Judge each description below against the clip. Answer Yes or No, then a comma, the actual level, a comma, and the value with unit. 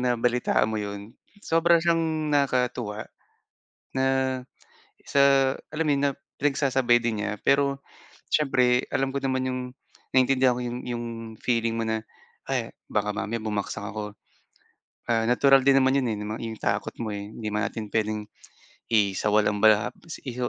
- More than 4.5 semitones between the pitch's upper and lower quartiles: No, average, 3.9 semitones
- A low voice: Yes, low, 120 Hz